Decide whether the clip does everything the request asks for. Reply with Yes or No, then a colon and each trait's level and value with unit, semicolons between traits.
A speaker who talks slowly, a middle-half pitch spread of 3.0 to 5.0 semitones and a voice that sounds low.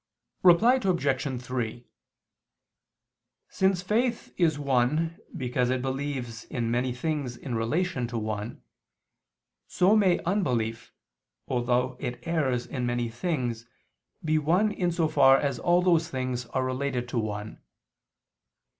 No: slow, 125 wpm; wide, 5.6 semitones; low, 130 Hz